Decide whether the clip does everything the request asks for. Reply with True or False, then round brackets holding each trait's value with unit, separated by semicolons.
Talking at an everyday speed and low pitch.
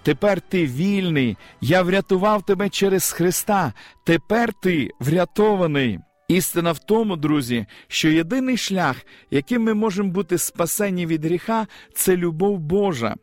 False (125 wpm; 180 Hz)